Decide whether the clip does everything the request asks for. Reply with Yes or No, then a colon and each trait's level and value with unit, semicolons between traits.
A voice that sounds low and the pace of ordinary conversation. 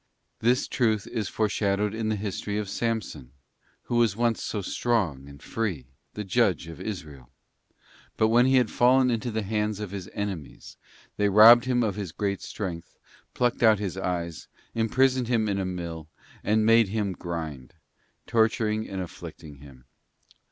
Yes: low, 105 Hz; average, 160 wpm